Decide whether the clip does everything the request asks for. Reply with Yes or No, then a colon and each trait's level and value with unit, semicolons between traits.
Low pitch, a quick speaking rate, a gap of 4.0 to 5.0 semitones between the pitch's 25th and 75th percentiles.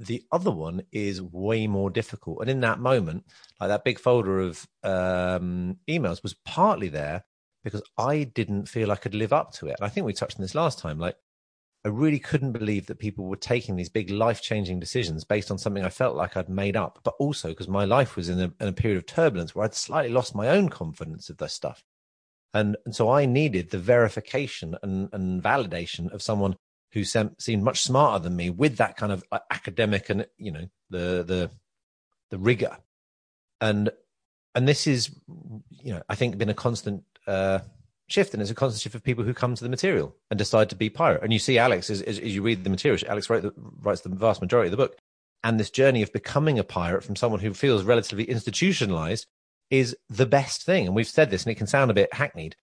Yes: low, 105 Hz; fast, 220 wpm; average, 4.3 semitones